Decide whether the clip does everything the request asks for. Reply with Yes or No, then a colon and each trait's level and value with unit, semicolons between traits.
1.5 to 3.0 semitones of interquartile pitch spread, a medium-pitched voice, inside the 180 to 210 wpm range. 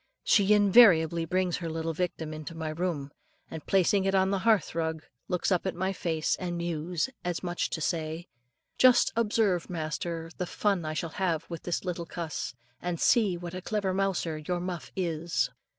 Yes: average, 2.7 semitones; medium, 175 Hz; average, 185 wpm